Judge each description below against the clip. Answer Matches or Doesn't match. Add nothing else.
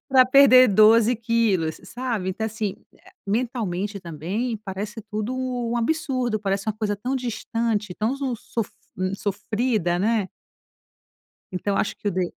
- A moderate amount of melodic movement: Matches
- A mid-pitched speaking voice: Doesn't match